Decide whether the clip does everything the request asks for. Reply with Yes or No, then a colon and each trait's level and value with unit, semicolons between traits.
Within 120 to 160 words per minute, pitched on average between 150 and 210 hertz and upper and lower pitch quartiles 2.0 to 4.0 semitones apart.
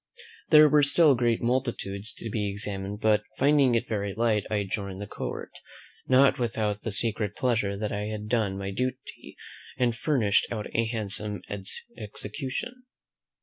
No: average, 150 wpm; low, 110 Hz; average, 3.5 semitones